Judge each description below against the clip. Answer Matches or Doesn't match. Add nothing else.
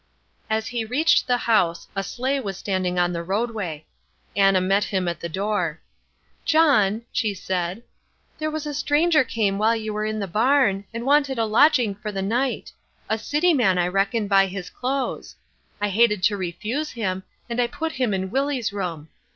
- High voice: Matches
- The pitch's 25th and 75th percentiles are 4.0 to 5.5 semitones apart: Matches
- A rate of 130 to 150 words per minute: Doesn't match